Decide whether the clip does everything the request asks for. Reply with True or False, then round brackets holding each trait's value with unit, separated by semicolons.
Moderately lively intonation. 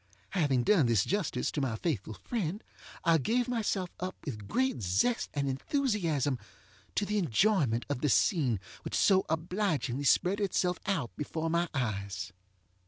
False (7.9 semitones)